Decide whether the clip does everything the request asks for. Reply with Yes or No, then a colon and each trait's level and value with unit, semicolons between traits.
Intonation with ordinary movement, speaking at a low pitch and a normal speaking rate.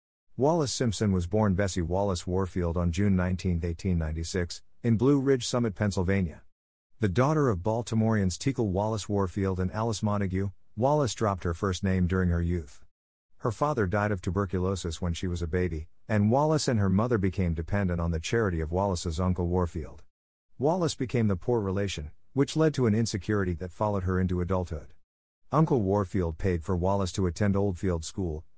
Yes: average, 3.6 semitones; very low, 95 Hz; average, 170 wpm